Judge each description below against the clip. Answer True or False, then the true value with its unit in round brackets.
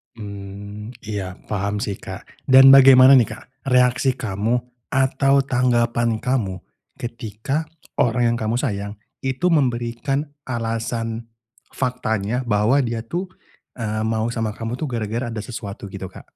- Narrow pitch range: False (3.2 semitones)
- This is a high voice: False (115 Hz)